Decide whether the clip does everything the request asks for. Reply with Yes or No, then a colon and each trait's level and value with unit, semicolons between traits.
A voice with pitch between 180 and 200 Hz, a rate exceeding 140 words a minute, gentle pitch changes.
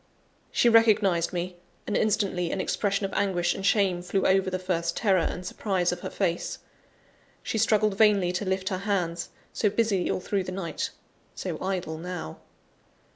Yes: high, 190 Hz; average, 170 wpm; narrow, 2.2 semitones